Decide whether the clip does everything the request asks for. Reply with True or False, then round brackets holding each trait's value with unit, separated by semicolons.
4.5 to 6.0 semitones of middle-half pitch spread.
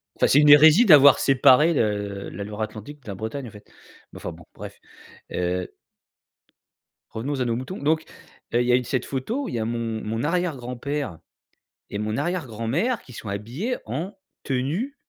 True (5.2 semitones)